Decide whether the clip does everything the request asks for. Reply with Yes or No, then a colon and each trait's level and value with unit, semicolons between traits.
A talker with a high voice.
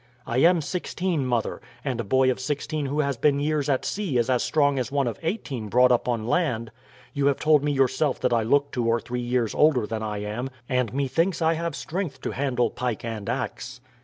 No: low, 130 Hz